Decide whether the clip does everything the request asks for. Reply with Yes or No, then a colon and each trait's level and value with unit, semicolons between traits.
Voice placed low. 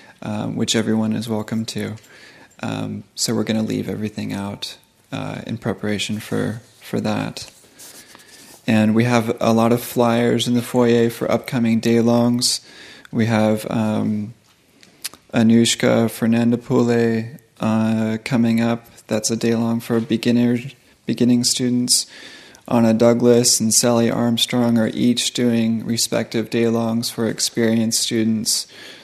Yes: low, 115 Hz